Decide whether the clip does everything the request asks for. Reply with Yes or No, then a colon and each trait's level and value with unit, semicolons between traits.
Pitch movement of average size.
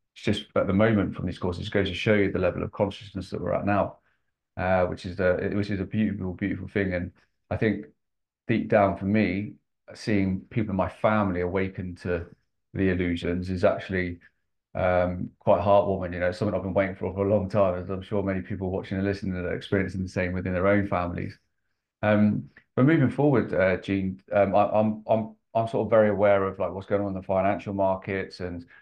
No: narrow, 2.2 semitones